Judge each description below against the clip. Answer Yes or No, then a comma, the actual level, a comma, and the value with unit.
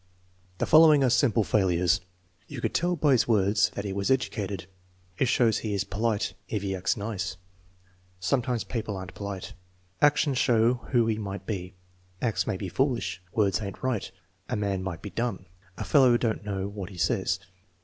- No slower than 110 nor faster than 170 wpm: No, average, 180 wpm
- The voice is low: Yes, low, 105 Hz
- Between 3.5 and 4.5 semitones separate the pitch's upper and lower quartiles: Yes, average, 3.8 semitones